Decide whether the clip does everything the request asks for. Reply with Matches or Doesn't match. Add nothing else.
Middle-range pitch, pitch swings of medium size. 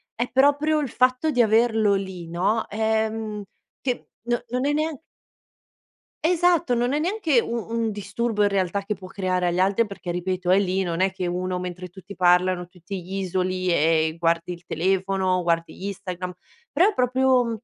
Doesn't match